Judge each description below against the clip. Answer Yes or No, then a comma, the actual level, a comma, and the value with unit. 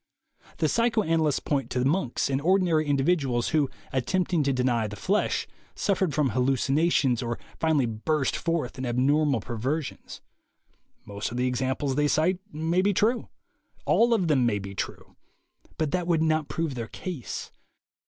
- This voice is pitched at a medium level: Yes, medium, 145 Hz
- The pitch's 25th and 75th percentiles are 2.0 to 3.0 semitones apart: No, average, 4.7 semitones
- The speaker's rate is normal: Yes, average, 155 wpm